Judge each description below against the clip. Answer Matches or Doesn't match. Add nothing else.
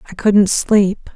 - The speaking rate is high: Doesn't match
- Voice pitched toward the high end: Matches